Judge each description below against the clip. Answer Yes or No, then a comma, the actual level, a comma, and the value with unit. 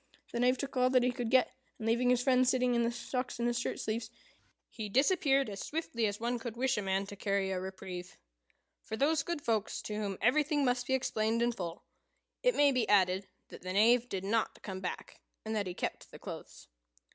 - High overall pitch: Yes, high, 235 Hz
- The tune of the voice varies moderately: Yes, average, 3.9 semitones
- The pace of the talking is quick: Yes, fast, 220 wpm